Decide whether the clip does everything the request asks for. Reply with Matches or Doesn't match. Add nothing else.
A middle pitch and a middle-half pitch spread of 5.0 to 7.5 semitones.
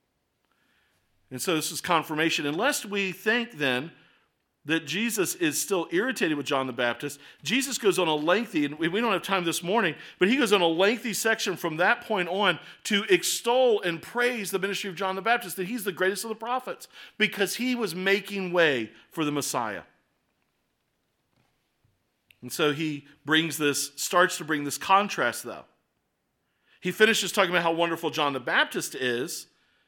Matches